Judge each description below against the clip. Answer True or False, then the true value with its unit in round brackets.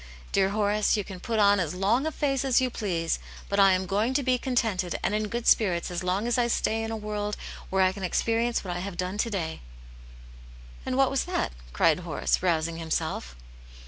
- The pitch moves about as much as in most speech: True (4.2 semitones)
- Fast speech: True (215 wpm)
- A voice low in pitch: False (205 Hz)